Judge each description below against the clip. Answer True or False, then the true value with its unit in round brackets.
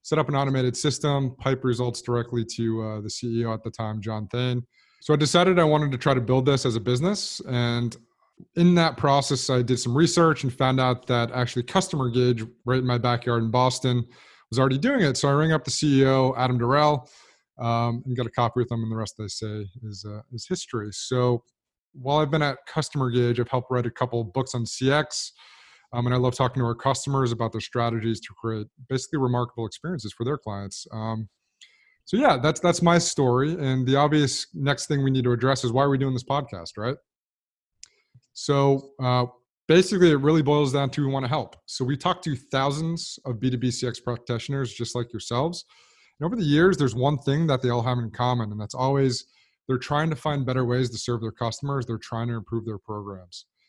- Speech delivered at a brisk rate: True (215 wpm)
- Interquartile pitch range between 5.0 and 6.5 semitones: False (3.0 semitones)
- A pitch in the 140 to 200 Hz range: False (125 Hz)